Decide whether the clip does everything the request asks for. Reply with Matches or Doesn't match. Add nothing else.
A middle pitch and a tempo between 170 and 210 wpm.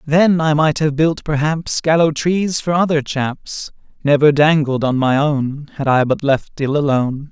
Matches